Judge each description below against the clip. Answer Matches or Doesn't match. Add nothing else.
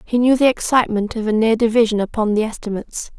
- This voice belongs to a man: Doesn't match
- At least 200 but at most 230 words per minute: Matches